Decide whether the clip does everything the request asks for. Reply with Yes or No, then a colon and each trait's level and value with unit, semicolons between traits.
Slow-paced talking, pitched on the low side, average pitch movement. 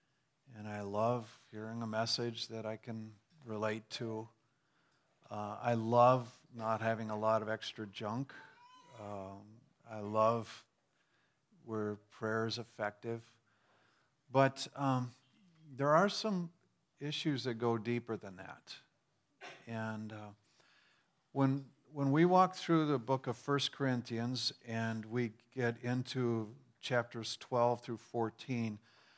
Yes: slow, 120 wpm; low, 120 Hz; average, 3.8 semitones